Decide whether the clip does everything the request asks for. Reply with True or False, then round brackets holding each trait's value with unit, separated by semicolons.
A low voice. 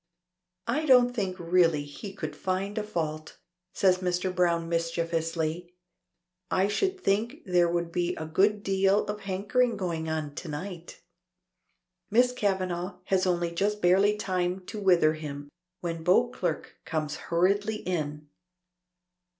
False (180 Hz)